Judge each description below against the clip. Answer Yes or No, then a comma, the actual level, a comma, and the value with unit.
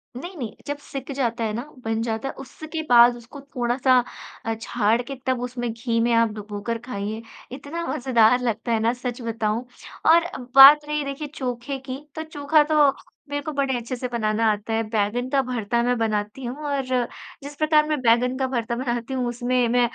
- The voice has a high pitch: Yes, high, 245 Hz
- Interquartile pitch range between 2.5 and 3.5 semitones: Yes, average, 3.1 semitones